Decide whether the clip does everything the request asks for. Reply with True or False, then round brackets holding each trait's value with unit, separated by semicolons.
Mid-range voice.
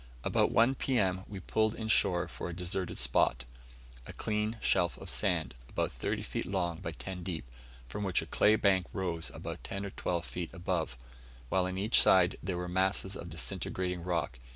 False (90 Hz)